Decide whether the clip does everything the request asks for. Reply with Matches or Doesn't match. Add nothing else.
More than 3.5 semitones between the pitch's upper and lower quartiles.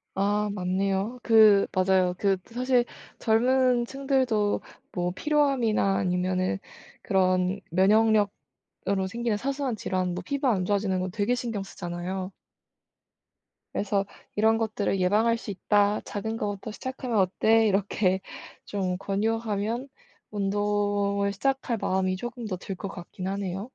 Doesn't match